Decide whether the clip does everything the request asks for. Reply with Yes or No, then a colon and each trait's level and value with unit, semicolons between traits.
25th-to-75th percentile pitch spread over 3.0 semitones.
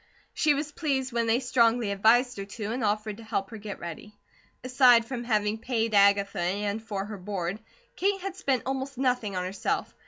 Yes: average, 3.8 semitones